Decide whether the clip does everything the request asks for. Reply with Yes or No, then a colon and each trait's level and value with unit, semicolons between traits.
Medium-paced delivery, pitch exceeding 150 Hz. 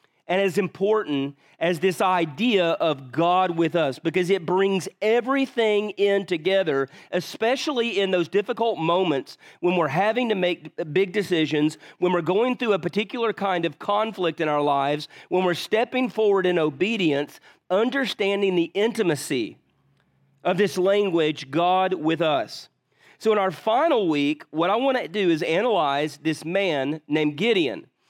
Yes: average, 150 wpm; medium, 185 Hz